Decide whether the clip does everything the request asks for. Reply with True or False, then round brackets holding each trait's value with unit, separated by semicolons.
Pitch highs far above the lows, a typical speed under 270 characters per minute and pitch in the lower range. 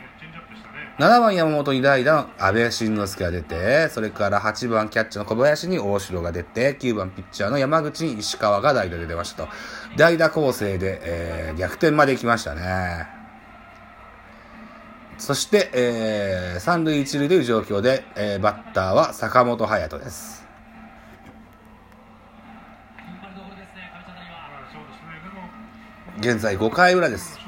True (6.8 semitones; 225 characters per minute; 110 Hz)